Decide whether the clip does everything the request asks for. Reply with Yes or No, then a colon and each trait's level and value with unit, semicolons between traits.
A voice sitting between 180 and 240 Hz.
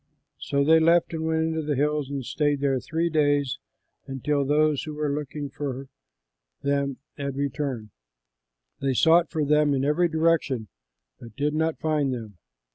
No: medium, 145 Hz